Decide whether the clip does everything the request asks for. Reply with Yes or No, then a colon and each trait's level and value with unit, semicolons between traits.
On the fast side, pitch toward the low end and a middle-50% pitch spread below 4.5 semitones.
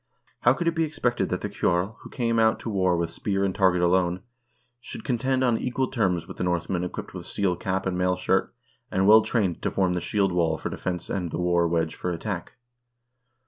Yes: fast, 220 wpm; very low, 95 Hz; average, 4.1 semitones